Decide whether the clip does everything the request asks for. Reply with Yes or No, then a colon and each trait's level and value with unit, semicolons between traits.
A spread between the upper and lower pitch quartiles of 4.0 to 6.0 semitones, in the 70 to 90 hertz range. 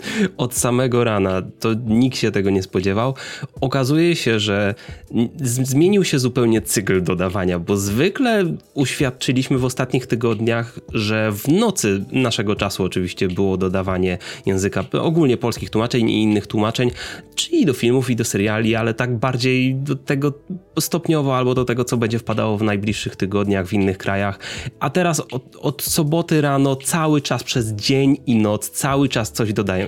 No: average, 4.7 semitones; low, 120 Hz